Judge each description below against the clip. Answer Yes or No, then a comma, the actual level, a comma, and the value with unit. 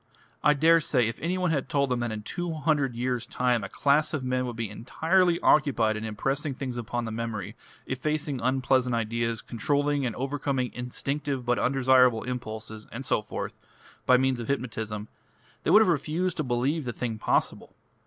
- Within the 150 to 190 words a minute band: Yes, average, 180 wpm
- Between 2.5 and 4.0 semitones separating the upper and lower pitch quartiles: Yes, average, 3.7 semitones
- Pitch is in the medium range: No, low, 130 Hz